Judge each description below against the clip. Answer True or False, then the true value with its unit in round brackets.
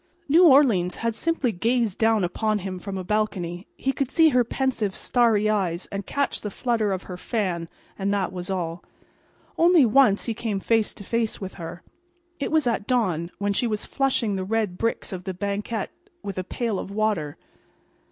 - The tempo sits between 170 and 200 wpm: True (190 wpm)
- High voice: True (210 Hz)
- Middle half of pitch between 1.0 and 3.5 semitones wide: False (4.0 semitones)